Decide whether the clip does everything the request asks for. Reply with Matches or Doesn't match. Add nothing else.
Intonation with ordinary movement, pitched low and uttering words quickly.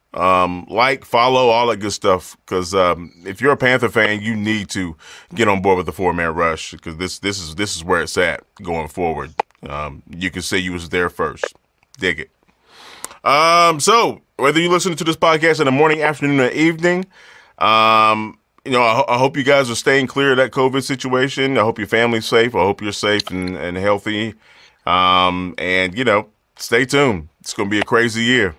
Doesn't match